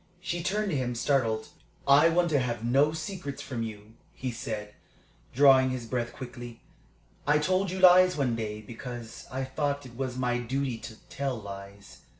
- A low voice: Yes, low, 130 Hz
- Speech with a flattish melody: No, average, 4.1 semitones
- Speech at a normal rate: Yes, average, 170 wpm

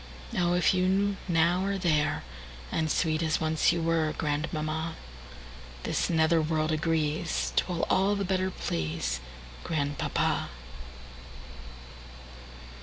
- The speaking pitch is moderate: Yes, medium, 155 Hz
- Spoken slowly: Yes, slow, 90 wpm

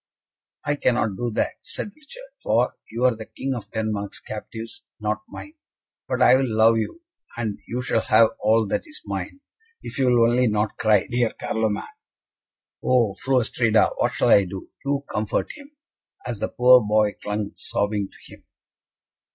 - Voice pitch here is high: No, low, 115 Hz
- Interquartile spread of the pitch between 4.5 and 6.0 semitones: No, average, 3.0 semitones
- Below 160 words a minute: No, average, 175 wpm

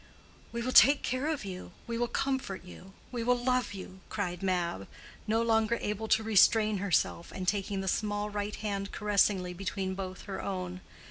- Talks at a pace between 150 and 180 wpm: Yes, average, 170 wpm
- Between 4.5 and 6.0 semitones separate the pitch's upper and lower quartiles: No, average, 3.2 semitones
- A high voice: Yes, high, 205 Hz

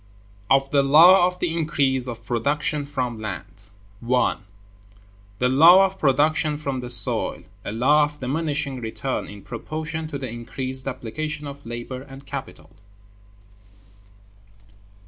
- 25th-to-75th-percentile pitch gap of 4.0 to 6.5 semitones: No, average, 3.5 semitones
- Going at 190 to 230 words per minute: No, slow, 135 wpm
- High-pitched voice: No, low, 135 Hz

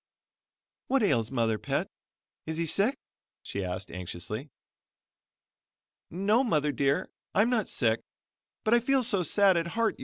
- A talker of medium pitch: Yes, medium, 170 Hz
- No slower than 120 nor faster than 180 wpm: Yes, average, 140 wpm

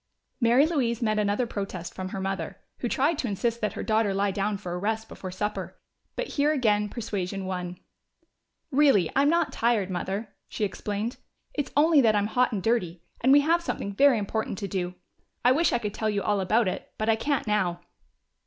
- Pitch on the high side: Yes, high, 215 Hz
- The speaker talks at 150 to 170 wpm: No, fast, 205 wpm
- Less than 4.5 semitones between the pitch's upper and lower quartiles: Yes, average, 4.1 semitones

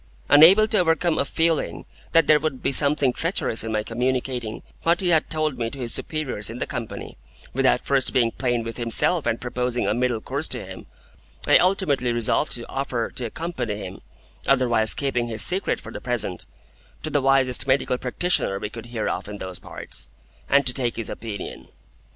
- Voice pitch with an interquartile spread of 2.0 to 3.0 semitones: No, average, 4.3 semitones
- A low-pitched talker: Yes, low, 125 Hz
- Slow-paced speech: No, average, 190 wpm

